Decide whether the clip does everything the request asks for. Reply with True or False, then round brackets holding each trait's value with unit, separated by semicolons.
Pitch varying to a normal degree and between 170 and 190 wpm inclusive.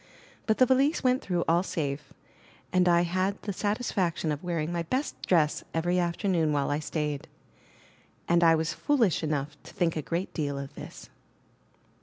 True (3.5 semitones; 175 wpm)